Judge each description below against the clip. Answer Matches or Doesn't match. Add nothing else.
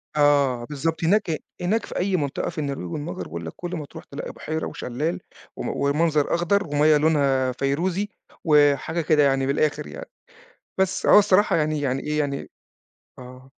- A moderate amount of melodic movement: Matches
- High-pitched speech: Doesn't match